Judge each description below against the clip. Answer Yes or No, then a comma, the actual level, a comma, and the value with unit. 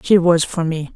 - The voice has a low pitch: No, medium, 170 Hz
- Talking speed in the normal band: No, fast, 250 wpm